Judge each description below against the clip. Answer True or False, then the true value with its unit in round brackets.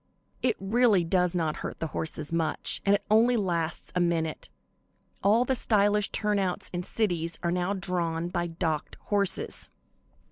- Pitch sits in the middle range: True (180 Hz)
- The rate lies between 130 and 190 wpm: True (150 wpm)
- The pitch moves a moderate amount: True (3.6 semitones)